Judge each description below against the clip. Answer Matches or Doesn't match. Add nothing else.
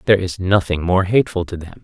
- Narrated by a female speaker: Doesn't match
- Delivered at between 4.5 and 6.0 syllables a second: Doesn't match